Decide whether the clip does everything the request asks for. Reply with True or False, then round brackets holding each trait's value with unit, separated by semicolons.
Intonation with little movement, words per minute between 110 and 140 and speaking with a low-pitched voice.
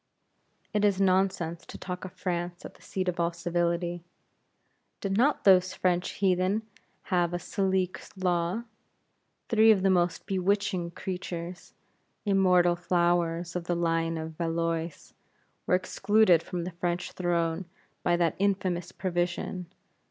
False (1.7 semitones; 135 wpm; 180 Hz)